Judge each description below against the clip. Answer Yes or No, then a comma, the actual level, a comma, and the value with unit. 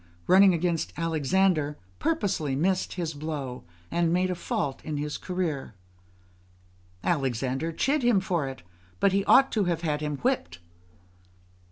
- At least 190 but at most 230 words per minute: No, average, 145 wpm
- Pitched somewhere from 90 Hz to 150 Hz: No, medium, 165 Hz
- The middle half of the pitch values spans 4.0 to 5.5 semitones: Yes, average, 4.3 semitones